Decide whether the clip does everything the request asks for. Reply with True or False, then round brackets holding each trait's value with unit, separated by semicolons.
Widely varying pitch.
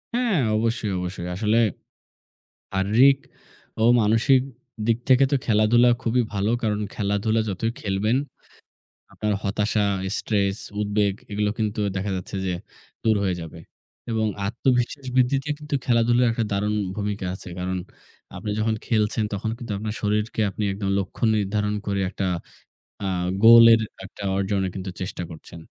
False (2.6 semitones)